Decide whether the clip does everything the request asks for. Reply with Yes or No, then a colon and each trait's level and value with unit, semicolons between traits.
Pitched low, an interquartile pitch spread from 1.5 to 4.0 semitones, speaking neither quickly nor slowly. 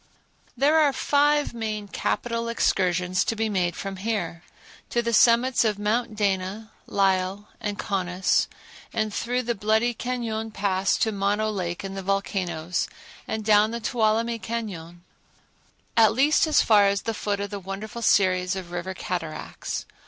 No: high, 210 Hz; average, 3.4 semitones; average, 150 wpm